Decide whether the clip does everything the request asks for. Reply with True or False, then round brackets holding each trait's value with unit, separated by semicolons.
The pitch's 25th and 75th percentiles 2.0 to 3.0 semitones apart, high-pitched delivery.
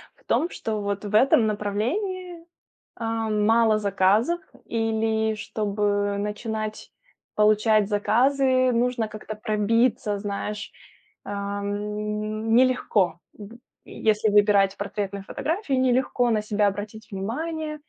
True (2.5 semitones; 215 Hz)